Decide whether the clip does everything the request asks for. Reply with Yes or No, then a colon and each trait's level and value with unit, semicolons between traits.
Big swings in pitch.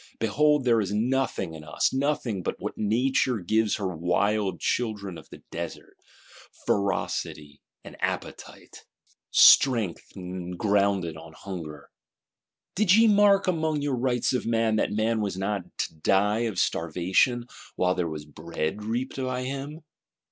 Yes: wide, 6.0 semitones